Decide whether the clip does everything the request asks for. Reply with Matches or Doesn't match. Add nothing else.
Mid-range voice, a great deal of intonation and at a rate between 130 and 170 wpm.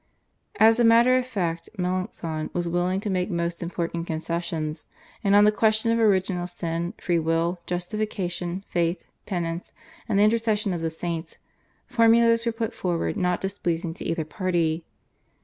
Doesn't match